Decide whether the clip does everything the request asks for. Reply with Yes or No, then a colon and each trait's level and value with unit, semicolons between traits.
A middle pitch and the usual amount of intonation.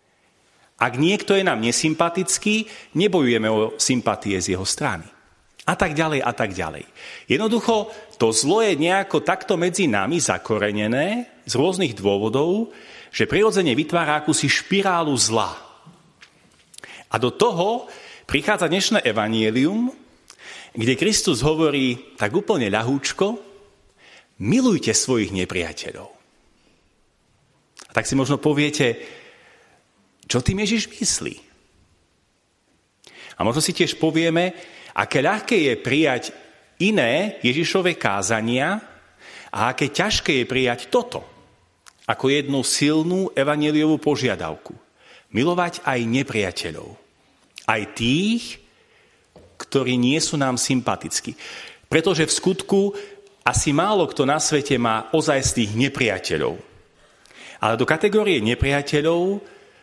No: medium, 150 Hz; wide, 8.5 semitones